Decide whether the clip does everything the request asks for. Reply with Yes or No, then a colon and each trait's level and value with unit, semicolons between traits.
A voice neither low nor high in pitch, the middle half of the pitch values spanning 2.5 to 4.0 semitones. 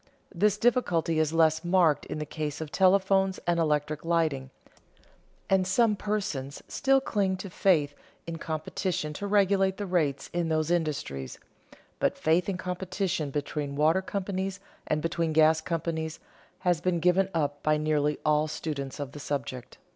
Yes: medium, 165 Hz; average, 3.7 semitones